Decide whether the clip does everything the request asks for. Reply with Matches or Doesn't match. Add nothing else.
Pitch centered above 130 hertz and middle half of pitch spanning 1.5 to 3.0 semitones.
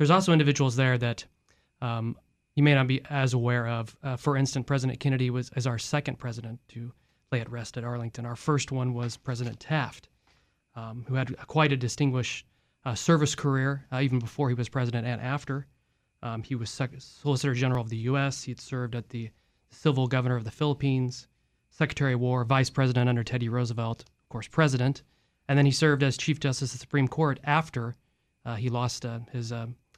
Doesn't match